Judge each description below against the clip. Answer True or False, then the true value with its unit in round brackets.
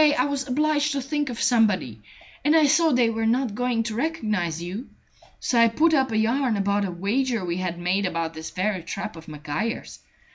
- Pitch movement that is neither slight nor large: False (6.6 semitones)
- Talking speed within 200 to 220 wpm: True (205 wpm)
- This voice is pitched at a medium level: False (225 Hz)